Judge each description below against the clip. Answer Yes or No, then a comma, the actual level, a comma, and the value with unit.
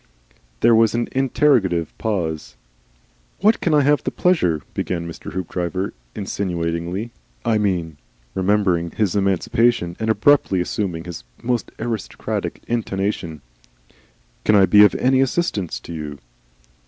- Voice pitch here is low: Yes, low, 100 Hz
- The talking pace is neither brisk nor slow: No, slow, 130 wpm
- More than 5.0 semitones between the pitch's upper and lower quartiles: Yes, wide, 5.4 semitones